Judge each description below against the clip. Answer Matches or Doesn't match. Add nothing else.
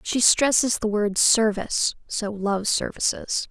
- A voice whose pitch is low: Doesn't match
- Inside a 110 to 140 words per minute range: Matches